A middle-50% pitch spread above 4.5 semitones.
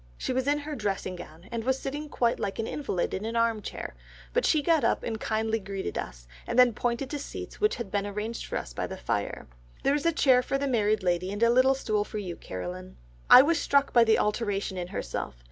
Yes: average, 5.2 semitones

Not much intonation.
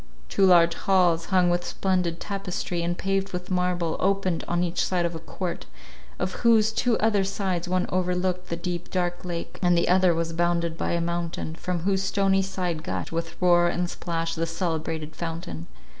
Yes: narrow, 1.8 semitones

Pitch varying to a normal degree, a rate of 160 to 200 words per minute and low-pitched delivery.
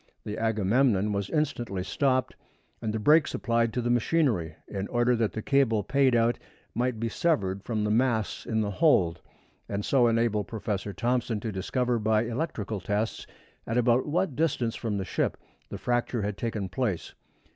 Yes: average, 3.2 semitones; average, 170 wpm; low, 115 Hz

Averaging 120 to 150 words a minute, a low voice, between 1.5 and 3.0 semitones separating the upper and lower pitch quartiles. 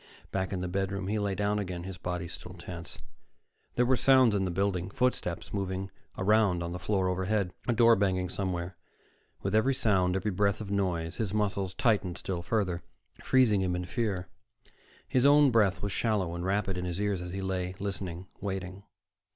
No: average, 185 wpm; very low, 95 Hz; narrow, 2.5 semitones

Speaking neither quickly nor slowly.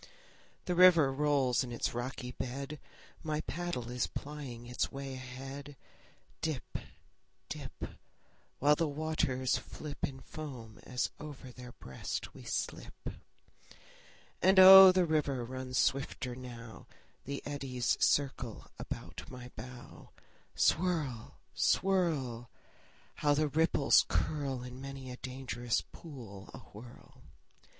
No: slow, 115 wpm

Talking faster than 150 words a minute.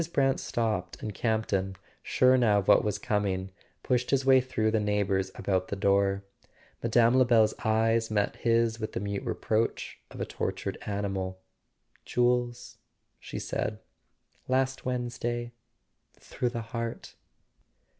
No: slow, 135 wpm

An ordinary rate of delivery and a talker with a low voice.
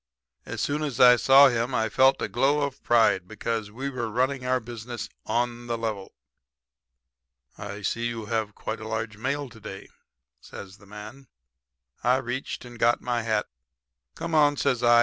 Yes: average, 175 wpm; low, 120 Hz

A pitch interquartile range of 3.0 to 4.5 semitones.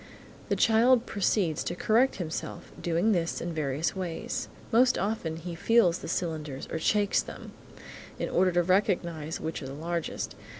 Yes: average, 4.2 semitones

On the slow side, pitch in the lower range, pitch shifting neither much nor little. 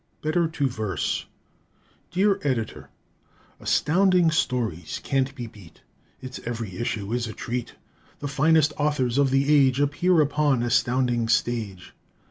Yes: slow, 125 wpm; low, 130 Hz; average, 4.2 semitones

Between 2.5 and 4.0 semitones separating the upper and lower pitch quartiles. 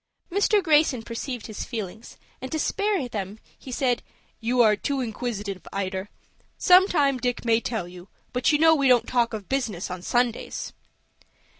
No: average, 4.7 semitones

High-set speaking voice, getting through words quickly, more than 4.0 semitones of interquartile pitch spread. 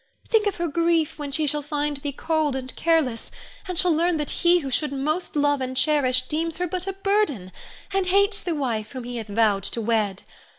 Yes: very high, 295 Hz; fast, 215 wpm; average, 5.0 semitones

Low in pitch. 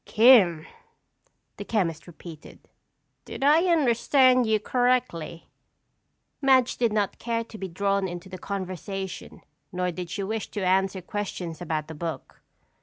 No: high, 195 Hz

